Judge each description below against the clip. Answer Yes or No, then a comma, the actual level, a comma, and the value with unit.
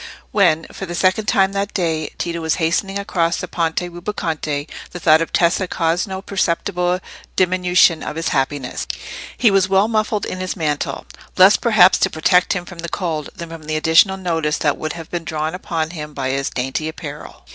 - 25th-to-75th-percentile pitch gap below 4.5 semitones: Yes, average, 3.0 semitones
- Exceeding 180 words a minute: Yes, average, 190 wpm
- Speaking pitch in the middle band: Yes, medium, 170 Hz